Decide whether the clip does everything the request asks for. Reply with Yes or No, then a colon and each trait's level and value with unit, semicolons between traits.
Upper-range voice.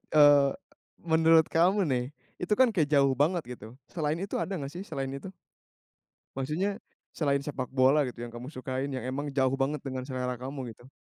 No: medium, 140 Hz